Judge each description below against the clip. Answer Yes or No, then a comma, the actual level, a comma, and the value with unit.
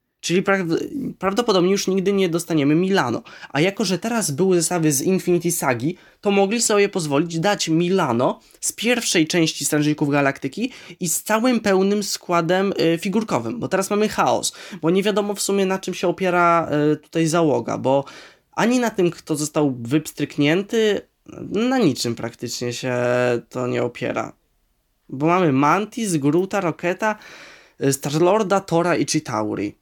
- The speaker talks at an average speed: Yes, average, 145 wpm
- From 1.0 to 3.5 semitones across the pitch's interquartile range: No, average, 4.8 semitones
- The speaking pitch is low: No, medium, 175 Hz